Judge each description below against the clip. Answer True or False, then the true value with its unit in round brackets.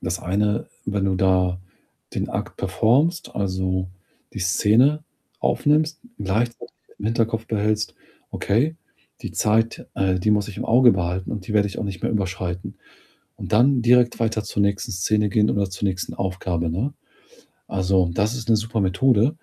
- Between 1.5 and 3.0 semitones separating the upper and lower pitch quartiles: False (3.5 semitones)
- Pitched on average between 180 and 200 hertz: False (105 Hz)